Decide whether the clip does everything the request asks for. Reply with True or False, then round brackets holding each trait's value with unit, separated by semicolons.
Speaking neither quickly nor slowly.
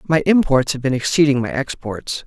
True (185 wpm)